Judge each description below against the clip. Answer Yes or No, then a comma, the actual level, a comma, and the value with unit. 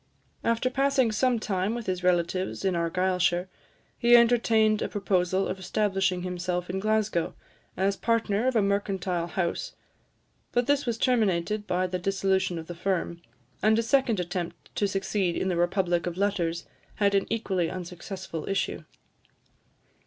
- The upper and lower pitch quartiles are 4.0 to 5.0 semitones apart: No, average, 3.3 semitones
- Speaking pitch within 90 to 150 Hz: No, high, 190 Hz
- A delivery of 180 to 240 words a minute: No, average, 150 wpm